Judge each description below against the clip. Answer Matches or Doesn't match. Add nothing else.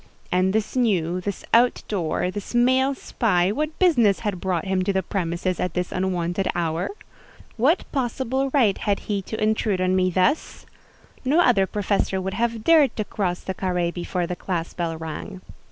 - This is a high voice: Matches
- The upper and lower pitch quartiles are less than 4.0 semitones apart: Doesn't match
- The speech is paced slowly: Doesn't match